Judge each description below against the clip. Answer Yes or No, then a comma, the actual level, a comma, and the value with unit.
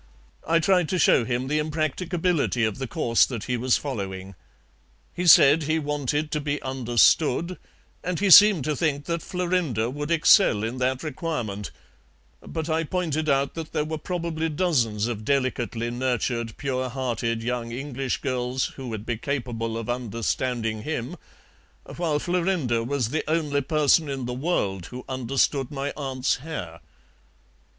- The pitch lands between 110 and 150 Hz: Yes, low, 135 Hz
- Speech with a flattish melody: No, average, 4.7 semitones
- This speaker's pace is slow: No, average, 155 wpm